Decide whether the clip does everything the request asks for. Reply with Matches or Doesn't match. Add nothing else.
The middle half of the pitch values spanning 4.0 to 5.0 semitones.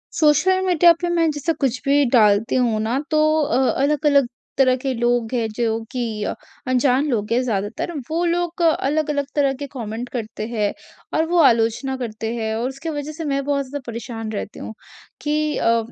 Matches